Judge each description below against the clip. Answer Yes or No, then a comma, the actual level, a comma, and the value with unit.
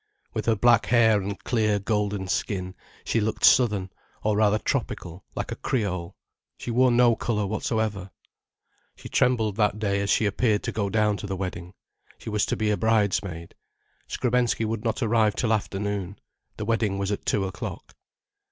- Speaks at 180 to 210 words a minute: No, average, 170 wpm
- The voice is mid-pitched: No, low, 105 Hz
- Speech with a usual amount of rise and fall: No, narrow, 2.2 semitones